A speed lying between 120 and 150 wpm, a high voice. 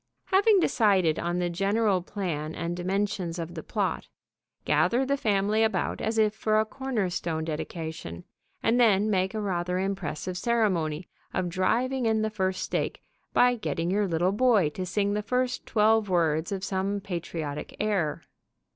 No: average, 160 wpm; high, 195 Hz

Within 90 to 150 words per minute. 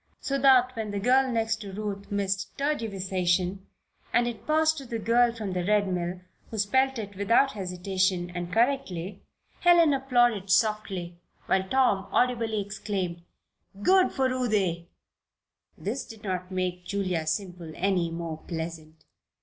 Yes: average, 140 wpm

